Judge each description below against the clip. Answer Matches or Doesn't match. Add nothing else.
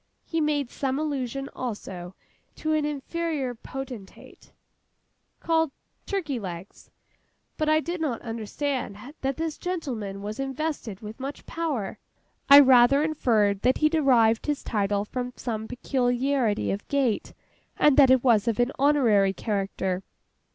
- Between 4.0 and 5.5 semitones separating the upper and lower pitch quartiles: Matches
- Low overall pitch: Doesn't match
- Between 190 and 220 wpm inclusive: Doesn't match